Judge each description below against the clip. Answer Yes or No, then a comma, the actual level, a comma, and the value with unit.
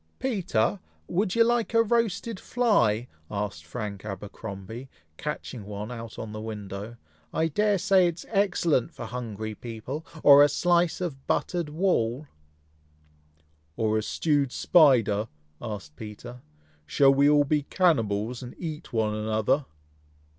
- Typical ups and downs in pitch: No, wide, 8.0 semitones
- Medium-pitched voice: No, low, 125 Hz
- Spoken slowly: Yes, slow, 130 wpm